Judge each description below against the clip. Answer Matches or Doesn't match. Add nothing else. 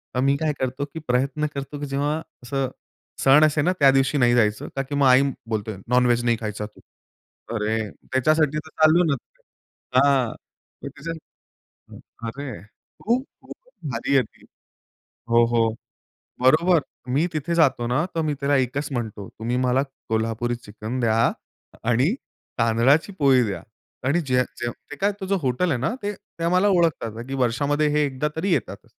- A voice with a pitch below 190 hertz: Matches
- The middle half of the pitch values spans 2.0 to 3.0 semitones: Doesn't match